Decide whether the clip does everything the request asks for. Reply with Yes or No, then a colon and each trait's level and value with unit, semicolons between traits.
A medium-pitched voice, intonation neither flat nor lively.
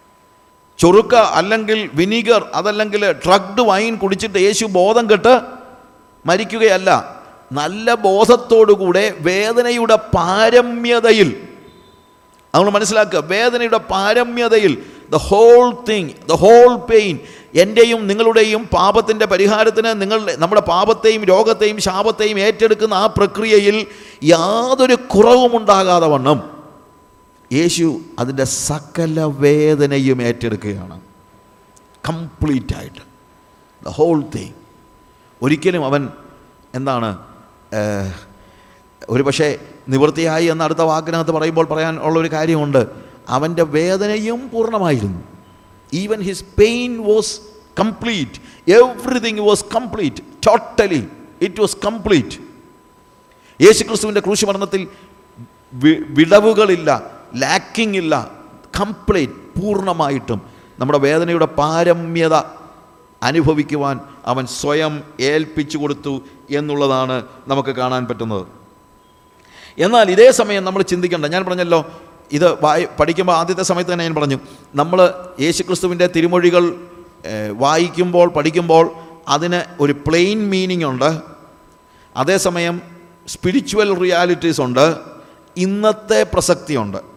No: medium, 175 Hz; wide, 6.4 semitones